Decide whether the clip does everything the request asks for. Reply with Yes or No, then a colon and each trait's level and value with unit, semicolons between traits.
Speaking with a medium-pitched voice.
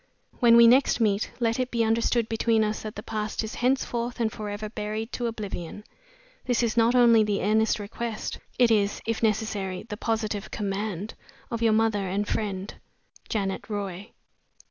No: high, 220 Hz